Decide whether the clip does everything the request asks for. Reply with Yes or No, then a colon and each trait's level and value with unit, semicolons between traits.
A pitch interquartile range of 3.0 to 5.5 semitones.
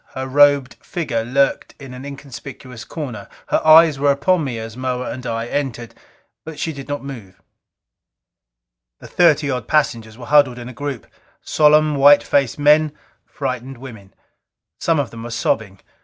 Yes: average, 3.3 semitones